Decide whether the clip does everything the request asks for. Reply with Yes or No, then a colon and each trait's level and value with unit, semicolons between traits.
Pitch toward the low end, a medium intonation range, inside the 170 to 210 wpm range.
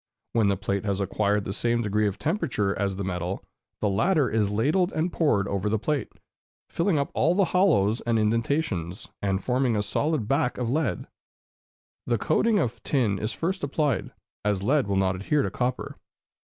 No: low, 115 Hz; wide, 7.0 semitones; average, 180 wpm